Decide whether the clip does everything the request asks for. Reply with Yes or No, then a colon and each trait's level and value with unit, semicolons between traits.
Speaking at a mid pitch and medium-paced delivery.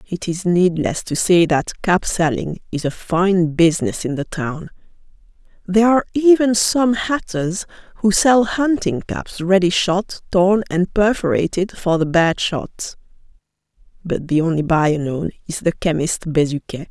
Yes: medium, 180 Hz; average, 150 wpm